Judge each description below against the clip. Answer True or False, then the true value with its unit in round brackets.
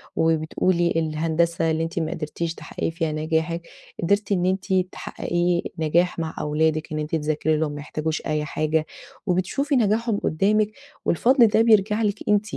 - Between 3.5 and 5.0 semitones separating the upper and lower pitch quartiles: True (4.1 semitones)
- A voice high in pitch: False (165 Hz)